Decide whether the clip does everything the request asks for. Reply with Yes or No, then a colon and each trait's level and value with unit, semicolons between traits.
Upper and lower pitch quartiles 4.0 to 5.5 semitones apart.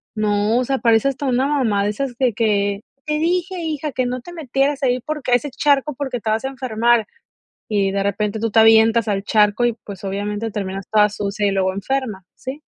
Yes: average, 4.5 semitones